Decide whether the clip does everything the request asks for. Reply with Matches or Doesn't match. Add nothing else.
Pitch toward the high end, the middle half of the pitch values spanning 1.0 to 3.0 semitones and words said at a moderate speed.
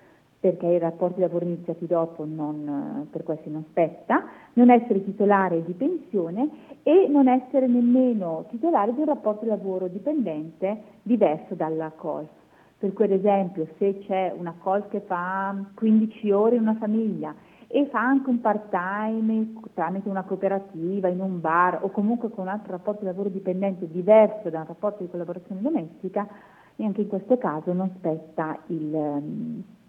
Doesn't match